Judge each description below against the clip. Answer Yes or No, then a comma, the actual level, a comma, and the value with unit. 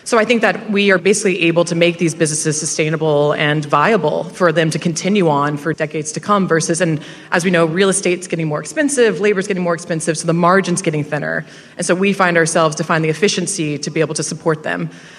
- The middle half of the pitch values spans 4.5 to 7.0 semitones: No, average, 3.0 semitones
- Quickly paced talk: Yes, fast, 230 wpm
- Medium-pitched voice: Yes, medium, 170 Hz